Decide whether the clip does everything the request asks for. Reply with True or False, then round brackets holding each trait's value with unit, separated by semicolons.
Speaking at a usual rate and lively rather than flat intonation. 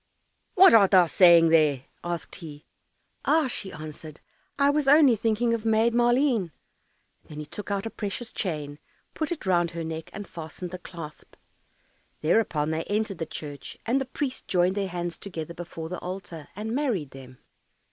True (170 wpm; 5.9 semitones)